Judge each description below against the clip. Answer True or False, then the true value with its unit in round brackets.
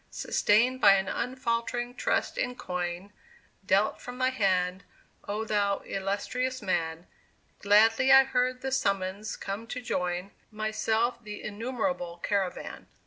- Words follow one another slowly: True (125 wpm)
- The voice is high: True (215 Hz)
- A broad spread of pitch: False (4.3 semitones)